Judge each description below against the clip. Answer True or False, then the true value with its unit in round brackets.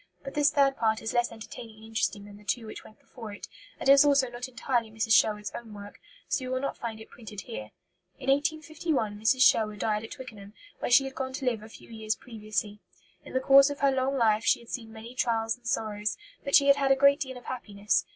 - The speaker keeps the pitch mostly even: False (3.7 semitones)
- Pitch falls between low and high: False (235 Hz)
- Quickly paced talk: True (240 wpm)